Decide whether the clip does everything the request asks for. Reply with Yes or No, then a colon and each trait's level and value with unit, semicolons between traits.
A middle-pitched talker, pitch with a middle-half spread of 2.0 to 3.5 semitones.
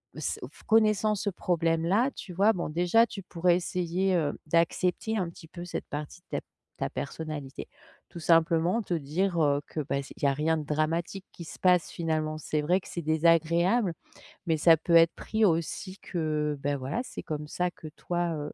Yes: medium, 170 Hz; average, 2.8 semitones